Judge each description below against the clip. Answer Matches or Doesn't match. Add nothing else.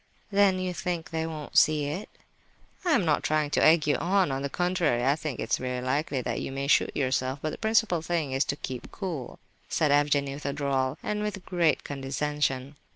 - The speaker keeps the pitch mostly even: Doesn't match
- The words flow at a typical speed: Doesn't match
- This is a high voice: Doesn't match